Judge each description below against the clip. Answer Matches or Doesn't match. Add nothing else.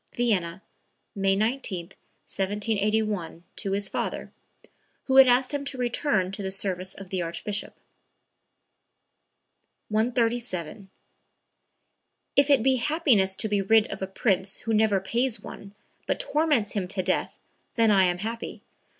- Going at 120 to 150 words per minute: Matches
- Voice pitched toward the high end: Matches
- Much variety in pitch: Doesn't match